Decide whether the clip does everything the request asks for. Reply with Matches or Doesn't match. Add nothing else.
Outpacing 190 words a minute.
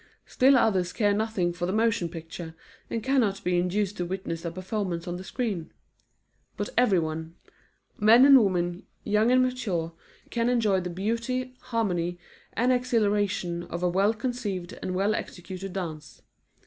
Doesn't match